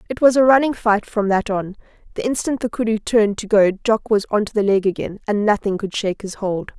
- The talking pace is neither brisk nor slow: No, fast, 250 wpm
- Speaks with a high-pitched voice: Yes, high, 215 Hz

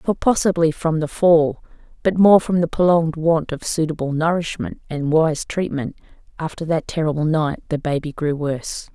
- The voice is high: No, medium, 160 Hz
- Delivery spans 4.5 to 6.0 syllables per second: Yes, 5.0 syllables/s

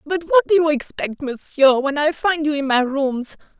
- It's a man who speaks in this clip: No, female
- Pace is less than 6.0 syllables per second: Yes, 4.6 syllables/s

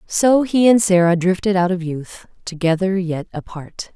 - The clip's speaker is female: Yes, female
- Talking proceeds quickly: No, average, 165 wpm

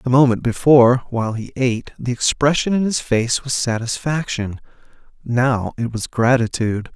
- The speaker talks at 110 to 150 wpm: Yes, average, 145 wpm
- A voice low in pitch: Yes, low, 125 Hz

